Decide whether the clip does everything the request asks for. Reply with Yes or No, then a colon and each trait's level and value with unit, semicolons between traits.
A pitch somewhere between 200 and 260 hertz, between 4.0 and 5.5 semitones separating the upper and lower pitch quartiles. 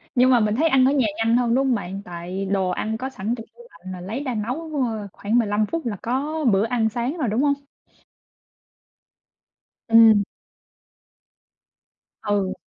Yes: high, 230 Hz; average, 4.3 semitones